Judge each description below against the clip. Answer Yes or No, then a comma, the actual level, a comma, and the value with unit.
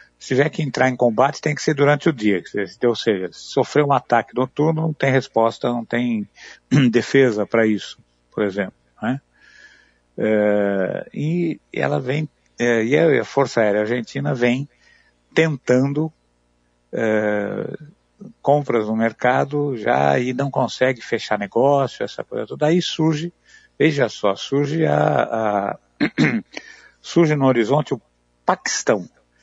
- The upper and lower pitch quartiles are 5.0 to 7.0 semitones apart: Yes, wide, 5.6 semitones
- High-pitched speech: No, low, 130 Hz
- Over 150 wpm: No, average, 130 wpm